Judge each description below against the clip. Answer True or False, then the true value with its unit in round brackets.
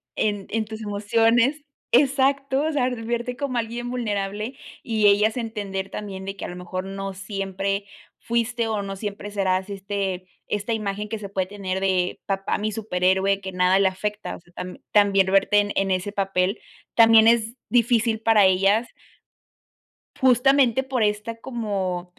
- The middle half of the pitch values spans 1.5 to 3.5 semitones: True (2.9 semitones)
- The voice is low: False (205 Hz)